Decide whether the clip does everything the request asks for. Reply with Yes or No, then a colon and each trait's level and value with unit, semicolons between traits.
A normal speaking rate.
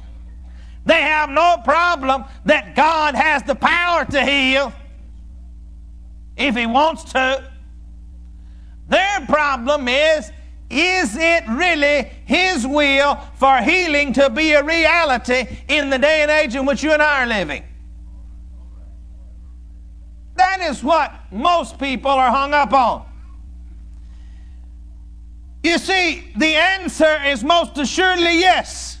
No: slow, 120 wpm